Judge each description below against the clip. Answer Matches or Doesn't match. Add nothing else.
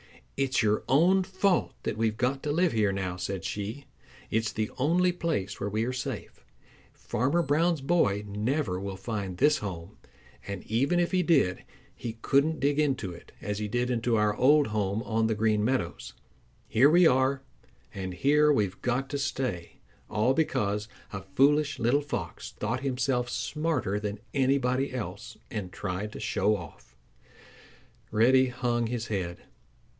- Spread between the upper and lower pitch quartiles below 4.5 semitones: Doesn't match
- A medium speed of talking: Matches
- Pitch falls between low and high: Doesn't match